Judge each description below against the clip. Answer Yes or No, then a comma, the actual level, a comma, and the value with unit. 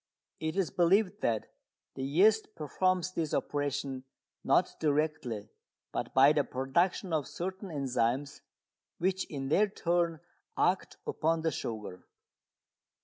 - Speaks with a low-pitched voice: No, medium, 155 Hz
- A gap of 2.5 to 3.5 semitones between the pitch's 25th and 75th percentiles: No, average, 5.3 semitones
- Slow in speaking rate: Yes, slow, 120 wpm